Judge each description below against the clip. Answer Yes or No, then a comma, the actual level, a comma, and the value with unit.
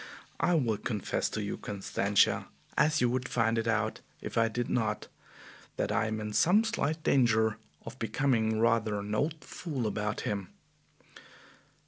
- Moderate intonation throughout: Yes, average, 3.3 semitones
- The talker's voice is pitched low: Yes, low, 115 Hz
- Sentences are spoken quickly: No, average, 155 wpm